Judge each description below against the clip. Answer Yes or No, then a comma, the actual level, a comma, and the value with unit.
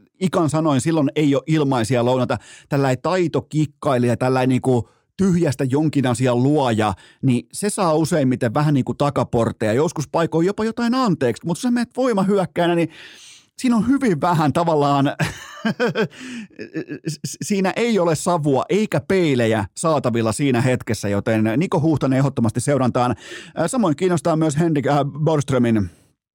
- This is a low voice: No, medium, 150 Hz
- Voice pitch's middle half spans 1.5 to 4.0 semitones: No, wide, 5.4 semitones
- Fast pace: No, average, 125 wpm